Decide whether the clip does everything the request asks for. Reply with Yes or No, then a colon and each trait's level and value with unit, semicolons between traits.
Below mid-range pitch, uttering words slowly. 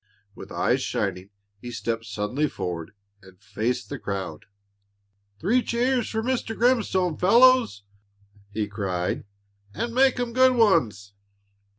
Yes: low, 125 Hz; slow, 120 wpm